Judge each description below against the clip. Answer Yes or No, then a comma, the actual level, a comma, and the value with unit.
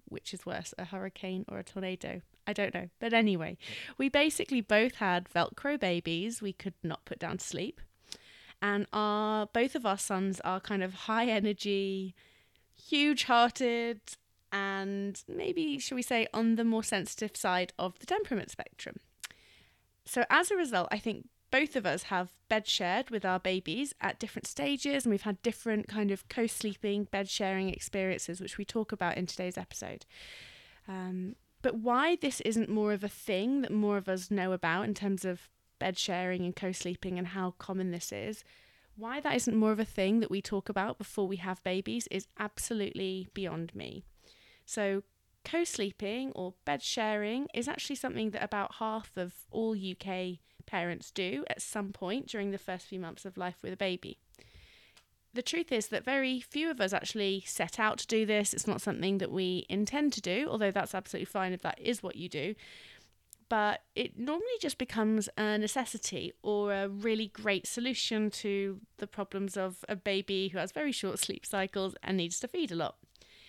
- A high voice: Yes, high, 205 Hz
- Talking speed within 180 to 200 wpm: Yes, average, 185 wpm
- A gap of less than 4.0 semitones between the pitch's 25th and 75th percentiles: Yes, average, 3.4 semitones